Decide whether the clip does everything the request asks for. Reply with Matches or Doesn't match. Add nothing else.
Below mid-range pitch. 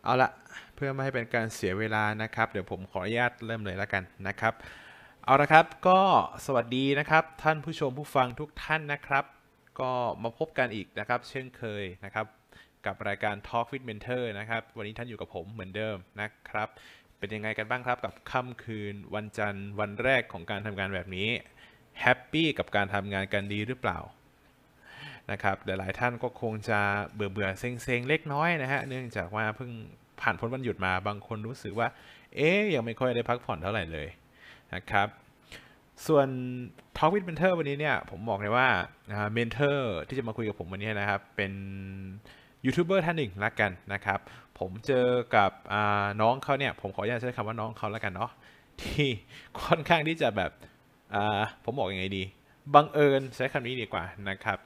Matches